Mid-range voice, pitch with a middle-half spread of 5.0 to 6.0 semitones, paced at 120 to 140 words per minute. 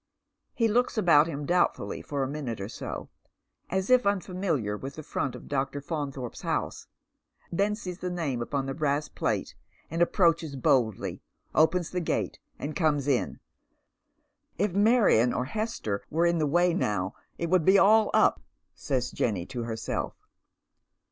No: medium, 155 Hz; average, 5.3 semitones; average, 170 wpm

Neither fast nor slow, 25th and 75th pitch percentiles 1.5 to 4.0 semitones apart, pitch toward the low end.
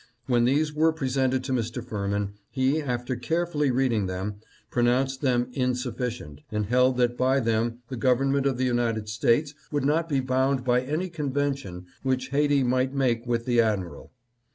Yes: average, 165 wpm; narrow, 2.6 semitones; low, 125 Hz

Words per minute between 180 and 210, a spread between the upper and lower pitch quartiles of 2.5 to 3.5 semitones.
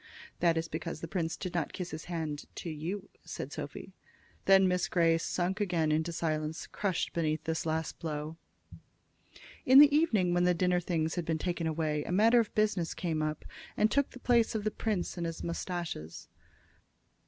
Yes: average, 185 wpm; average, 3.0 semitones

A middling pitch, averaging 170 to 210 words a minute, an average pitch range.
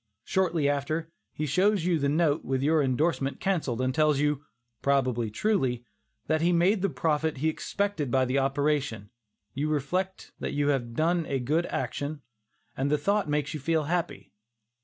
Yes: medium, 150 Hz; average, 175 wpm; average, 3.5 semitones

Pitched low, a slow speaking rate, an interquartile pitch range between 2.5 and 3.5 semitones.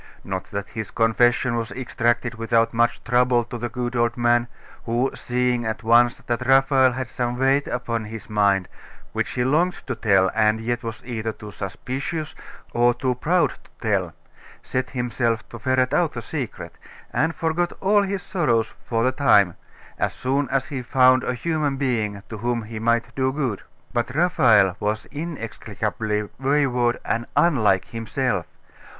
No: low, 120 Hz; average, 165 wpm; average, 2.8 semitones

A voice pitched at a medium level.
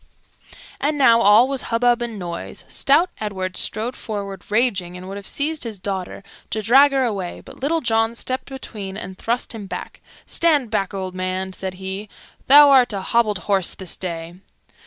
No: high, 215 Hz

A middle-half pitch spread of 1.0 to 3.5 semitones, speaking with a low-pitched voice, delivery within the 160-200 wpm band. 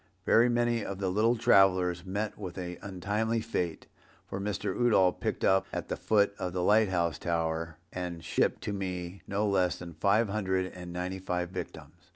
Yes: narrow, 2.6 semitones; very low, 95 Hz; average, 185 wpm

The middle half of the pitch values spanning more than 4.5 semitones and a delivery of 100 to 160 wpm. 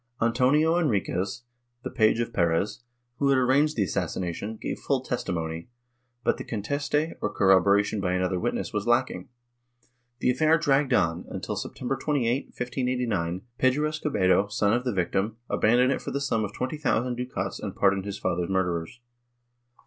Yes: wide, 5.5 semitones; average, 155 wpm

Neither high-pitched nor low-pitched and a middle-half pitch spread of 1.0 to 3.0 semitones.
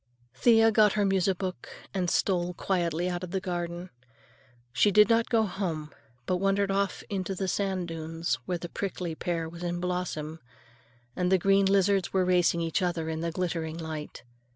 Yes: medium, 180 Hz; narrow, 2.5 semitones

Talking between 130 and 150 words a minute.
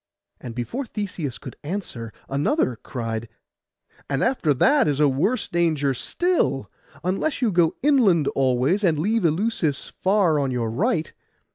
Yes: average, 140 wpm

